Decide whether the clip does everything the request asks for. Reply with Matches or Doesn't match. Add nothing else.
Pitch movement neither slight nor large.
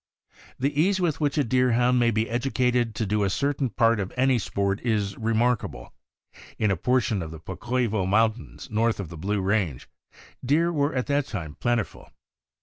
Matches